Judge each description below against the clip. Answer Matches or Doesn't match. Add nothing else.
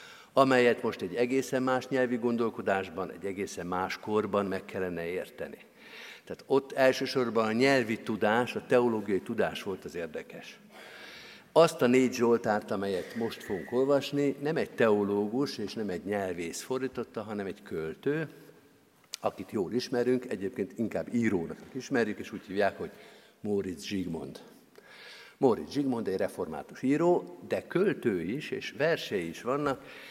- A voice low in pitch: Matches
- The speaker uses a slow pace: Doesn't match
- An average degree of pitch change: Matches